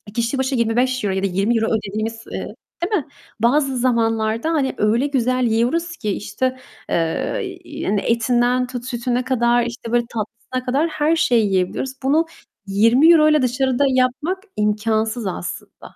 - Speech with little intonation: No, average, 3.1 semitones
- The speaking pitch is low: No, high, 245 Hz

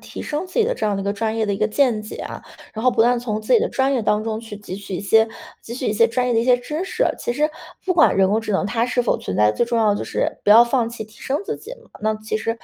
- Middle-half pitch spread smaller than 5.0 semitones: Yes, average, 2.8 semitones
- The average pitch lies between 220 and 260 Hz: Yes, high, 225 Hz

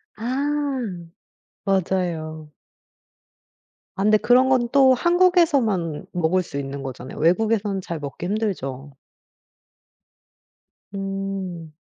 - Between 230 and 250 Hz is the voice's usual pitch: No, high, 195 Hz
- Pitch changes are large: Yes, wide, 7.2 semitones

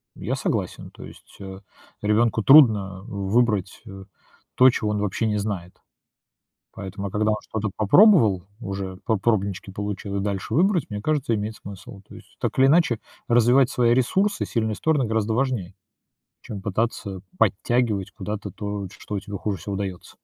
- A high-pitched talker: No, low, 105 Hz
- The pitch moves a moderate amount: Yes, average, 3.2 semitones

